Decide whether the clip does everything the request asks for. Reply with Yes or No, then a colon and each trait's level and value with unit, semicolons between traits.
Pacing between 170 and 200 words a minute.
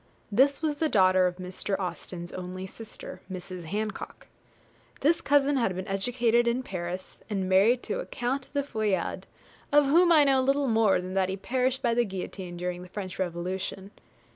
Yes: average, 175 wpm